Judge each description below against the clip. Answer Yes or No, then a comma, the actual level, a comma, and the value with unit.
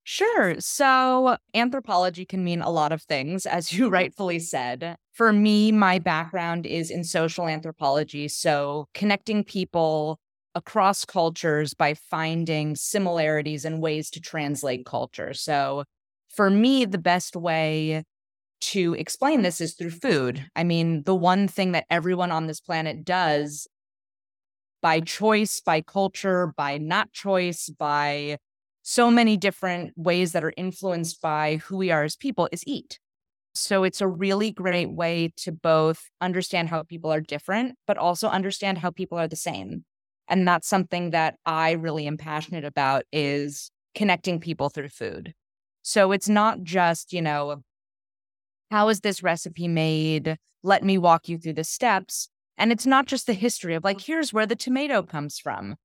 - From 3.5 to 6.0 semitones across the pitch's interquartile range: Yes, average, 3.8 semitones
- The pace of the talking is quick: No, average, 160 wpm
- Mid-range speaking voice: Yes, medium, 170 Hz